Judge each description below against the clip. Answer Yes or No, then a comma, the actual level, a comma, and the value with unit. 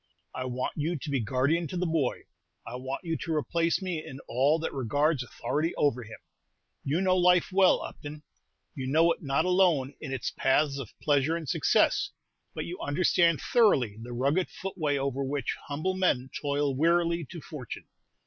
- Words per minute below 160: No, average, 175 wpm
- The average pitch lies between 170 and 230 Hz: No, medium, 150 Hz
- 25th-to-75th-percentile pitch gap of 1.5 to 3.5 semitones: No, average, 4.1 semitones